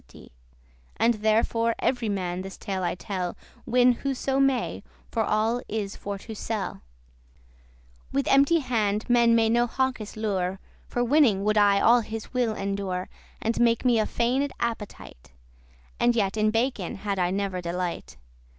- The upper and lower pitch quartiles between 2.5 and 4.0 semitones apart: Yes, average, 3.4 semitones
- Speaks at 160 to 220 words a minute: Yes, average, 165 wpm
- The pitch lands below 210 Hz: No, high, 220 Hz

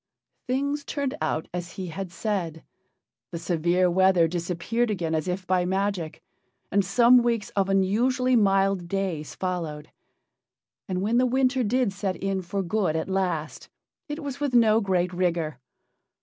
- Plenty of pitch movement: No, average, 4.7 semitones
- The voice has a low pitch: No, high, 190 Hz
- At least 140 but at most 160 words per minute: Yes, average, 150 wpm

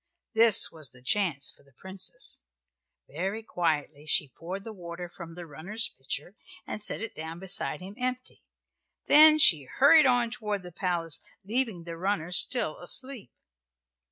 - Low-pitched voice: No, medium, 185 Hz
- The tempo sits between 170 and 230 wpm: No, average, 155 wpm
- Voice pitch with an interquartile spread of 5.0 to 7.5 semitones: Yes, wide, 5.4 semitones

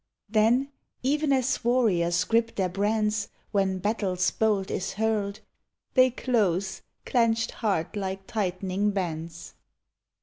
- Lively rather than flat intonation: No, average, 3.2 semitones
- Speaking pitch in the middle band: No, high, 210 Hz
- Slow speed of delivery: Yes, slow, 110 wpm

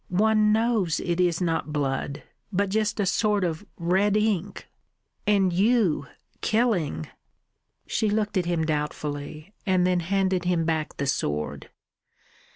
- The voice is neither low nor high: Yes, medium, 180 Hz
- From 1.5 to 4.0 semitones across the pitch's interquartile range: No, average, 4.6 semitones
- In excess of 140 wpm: No, slow, 135 wpm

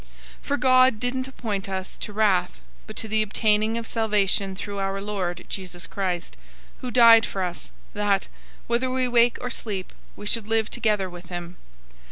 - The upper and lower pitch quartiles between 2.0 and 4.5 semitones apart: Yes, average, 3.4 semitones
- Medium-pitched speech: No, high, 210 Hz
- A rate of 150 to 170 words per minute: No, average, 180 wpm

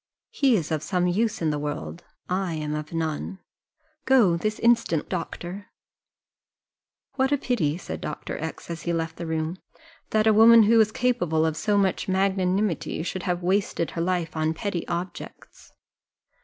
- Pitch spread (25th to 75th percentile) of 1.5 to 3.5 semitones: No, average, 4.6 semitones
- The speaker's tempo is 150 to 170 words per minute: Yes, average, 165 wpm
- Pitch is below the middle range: No, medium, 180 Hz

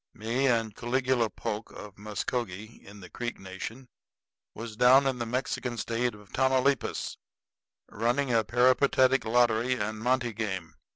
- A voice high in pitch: No, low, 120 Hz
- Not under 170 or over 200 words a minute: No, slow, 135 wpm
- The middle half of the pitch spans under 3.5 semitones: Yes, average, 2.9 semitones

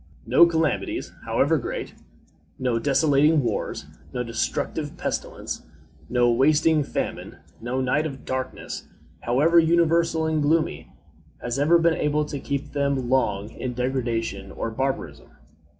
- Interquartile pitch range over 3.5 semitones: Yes, average, 4.3 semitones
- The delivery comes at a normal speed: No, slow, 125 wpm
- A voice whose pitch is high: No, medium, 140 Hz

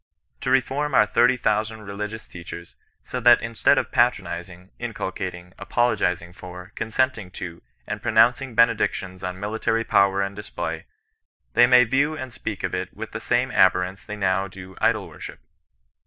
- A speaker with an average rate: Yes, average, 155 wpm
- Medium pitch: No, low, 105 Hz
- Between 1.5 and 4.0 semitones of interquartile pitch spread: No, average, 4.4 semitones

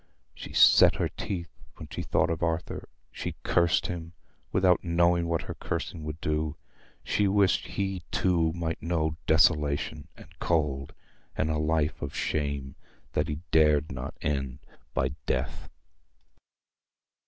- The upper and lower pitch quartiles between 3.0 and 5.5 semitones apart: No, narrow, 2.5 semitones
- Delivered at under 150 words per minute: Yes, average, 140 wpm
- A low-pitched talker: Yes, very low, 80 Hz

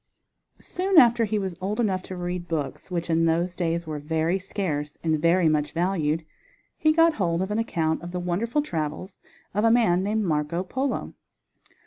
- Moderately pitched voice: Yes, medium, 180 Hz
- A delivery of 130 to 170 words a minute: No, average, 180 wpm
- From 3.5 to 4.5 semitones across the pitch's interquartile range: Yes, average, 4.2 semitones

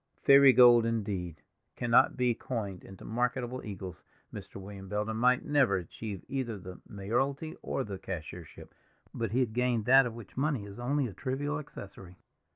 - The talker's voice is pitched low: Yes, low, 115 Hz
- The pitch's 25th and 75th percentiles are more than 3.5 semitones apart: Yes, average, 4.6 semitones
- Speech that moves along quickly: No, average, 165 wpm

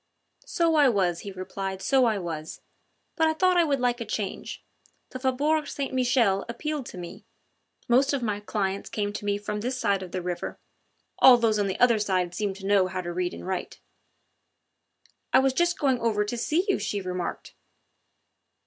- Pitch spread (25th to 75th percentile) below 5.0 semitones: No, wide, 5.5 semitones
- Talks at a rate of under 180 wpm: No, average, 195 wpm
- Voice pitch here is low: No, high, 210 Hz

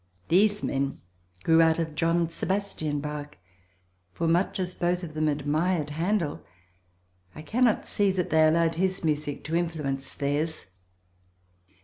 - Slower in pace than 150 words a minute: Yes, slow, 135 wpm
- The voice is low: No, medium, 165 Hz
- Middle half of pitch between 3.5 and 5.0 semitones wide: No, average, 3.0 semitones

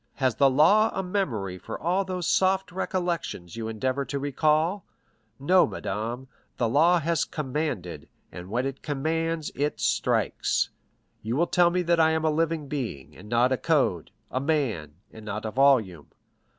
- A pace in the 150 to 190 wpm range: Yes, average, 165 wpm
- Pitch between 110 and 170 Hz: Yes, medium, 140 Hz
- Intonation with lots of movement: Yes, wide, 6.8 semitones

